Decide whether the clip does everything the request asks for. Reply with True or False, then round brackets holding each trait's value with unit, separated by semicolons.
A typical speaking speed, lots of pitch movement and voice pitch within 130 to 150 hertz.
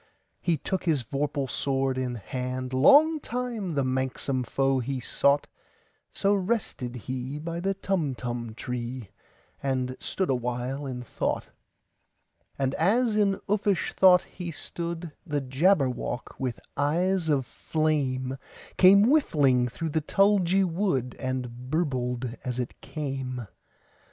False (105 wpm; 5.9 semitones; 140 Hz)